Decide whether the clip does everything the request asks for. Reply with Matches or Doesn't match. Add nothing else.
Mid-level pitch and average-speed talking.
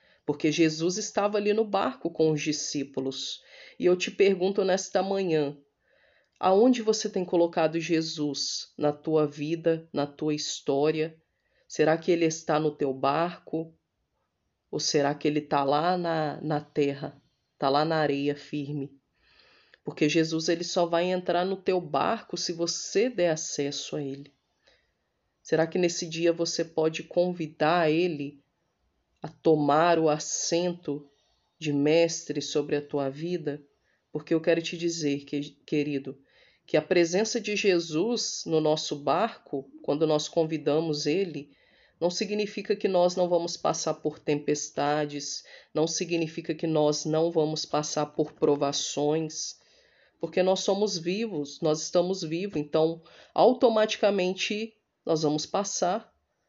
Matches